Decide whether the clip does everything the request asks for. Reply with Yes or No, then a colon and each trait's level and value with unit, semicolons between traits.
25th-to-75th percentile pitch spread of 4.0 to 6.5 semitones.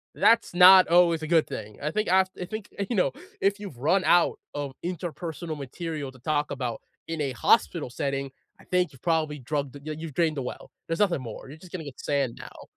Yes: average, 4.4 semitones